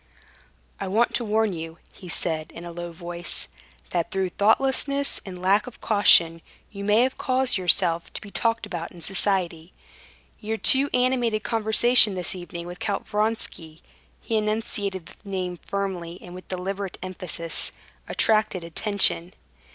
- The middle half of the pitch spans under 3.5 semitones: No, average, 3.9 semitones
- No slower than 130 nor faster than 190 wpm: Yes, average, 145 wpm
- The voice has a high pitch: Yes, high, 195 Hz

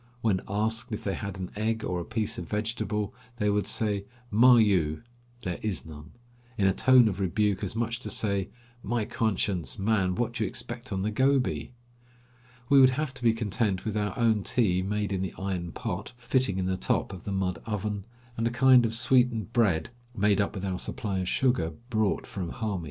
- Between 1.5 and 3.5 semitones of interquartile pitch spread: Yes, average, 3.1 semitones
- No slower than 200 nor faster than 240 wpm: Yes, fast, 205 wpm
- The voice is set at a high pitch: No, low, 105 Hz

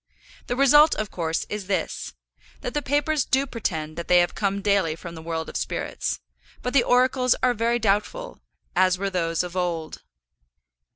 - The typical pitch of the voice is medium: No, high, 200 Hz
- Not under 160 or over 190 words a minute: Yes, average, 175 wpm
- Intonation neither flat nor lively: No, wide, 6.5 semitones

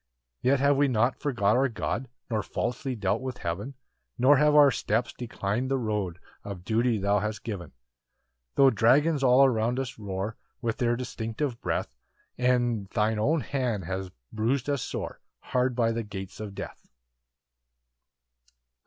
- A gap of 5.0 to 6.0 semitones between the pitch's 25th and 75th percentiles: No, average, 3.7 semitones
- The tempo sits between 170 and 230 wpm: No, average, 160 wpm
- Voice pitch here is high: No, low, 120 Hz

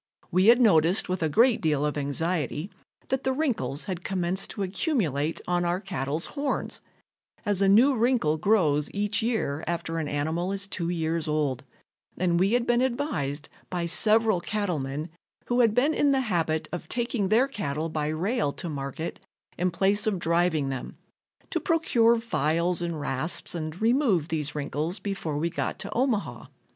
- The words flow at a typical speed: Yes, average, 170 wpm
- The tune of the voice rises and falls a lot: Yes, wide, 6.0 semitones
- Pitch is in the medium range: Yes, medium, 175 Hz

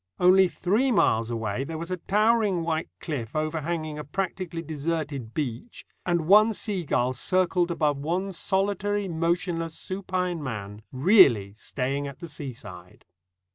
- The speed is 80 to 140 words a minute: Yes, slow, 135 wpm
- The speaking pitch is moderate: Yes, medium, 165 Hz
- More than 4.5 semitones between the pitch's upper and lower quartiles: Yes, average, 5.0 semitones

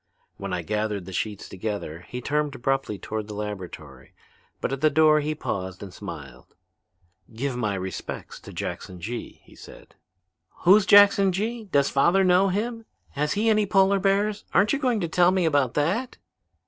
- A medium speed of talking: Yes, average, 175 wpm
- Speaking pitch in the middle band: Yes, medium, 145 Hz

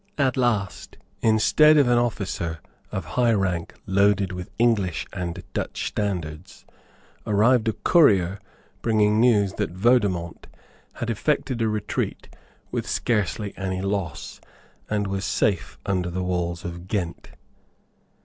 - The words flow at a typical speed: No, slow, 125 wpm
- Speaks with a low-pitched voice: Yes, low, 100 Hz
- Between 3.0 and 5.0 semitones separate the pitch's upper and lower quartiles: Yes, average, 3.8 semitones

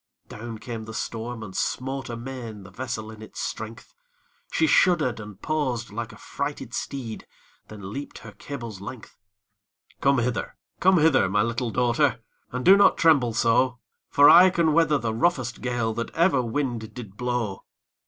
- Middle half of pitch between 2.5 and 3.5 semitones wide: No, average, 4.0 semitones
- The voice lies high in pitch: No, low, 120 Hz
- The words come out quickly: No, average, 165 wpm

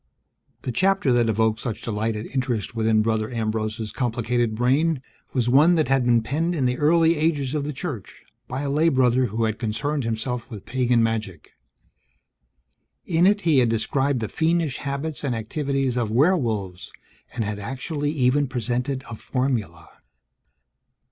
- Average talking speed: Yes, average, 160 wpm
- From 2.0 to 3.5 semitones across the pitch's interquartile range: No, average, 4.3 semitones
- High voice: No, low, 125 Hz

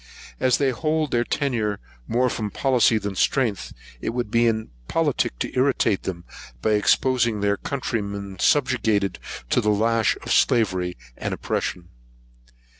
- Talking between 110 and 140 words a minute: Yes, slow, 135 wpm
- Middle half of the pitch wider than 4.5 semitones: No, average, 4.0 semitones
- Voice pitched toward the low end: Yes, low, 115 Hz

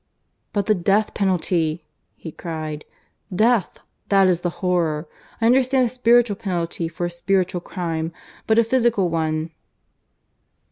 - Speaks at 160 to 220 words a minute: No, slow, 135 wpm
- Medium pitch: Yes, medium, 180 Hz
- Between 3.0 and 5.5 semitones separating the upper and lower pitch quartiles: Yes, average, 4.6 semitones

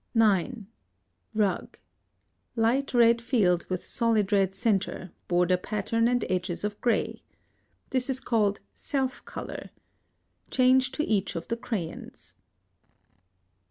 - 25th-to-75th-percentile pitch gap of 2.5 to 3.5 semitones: No, average, 4.2 semitones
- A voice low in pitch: No, high, 220 Hz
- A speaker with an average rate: No, slow, 115 wpm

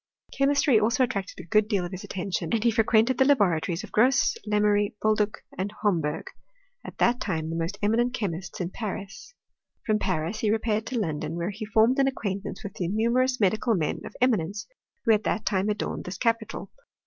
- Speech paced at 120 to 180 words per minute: No, average, 195 wpm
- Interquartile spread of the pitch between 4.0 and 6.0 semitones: No, average, 3.5 semitones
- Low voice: No, high, 210 Hz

